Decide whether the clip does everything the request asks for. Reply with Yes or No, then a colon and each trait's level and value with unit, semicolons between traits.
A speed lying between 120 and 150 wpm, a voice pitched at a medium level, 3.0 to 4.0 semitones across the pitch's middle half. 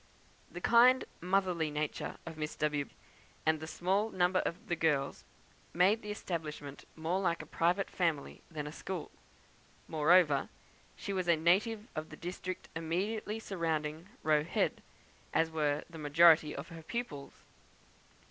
Yes: average, 145 wpm; medium, 165 Hz; average, 3.3 semitones